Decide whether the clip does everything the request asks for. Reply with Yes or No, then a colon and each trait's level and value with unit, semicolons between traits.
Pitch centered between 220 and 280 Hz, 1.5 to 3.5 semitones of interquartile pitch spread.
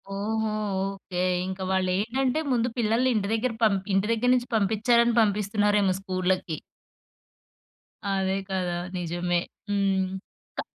No: high, 200 Hz; average, 2.9 semitones